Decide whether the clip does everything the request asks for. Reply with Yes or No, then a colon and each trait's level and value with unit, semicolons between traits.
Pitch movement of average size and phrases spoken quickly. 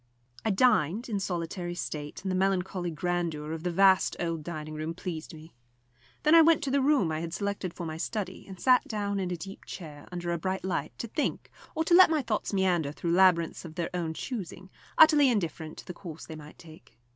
Yes: average, 3.7 semitones; fast, 215 wpm